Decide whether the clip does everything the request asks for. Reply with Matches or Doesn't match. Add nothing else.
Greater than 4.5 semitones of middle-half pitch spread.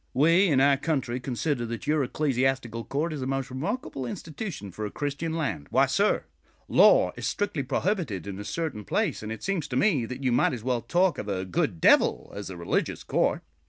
Matches